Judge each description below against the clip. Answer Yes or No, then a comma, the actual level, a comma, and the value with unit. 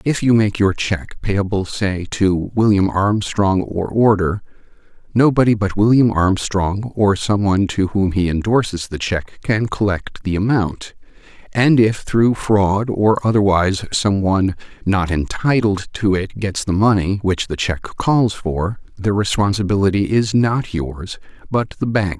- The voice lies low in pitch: Yes, low, 100 Hz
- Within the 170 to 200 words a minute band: No, average, 155 wpm